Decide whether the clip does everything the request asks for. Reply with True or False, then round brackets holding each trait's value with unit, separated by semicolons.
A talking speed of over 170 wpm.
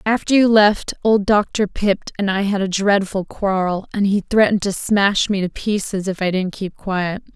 True (205 wpm)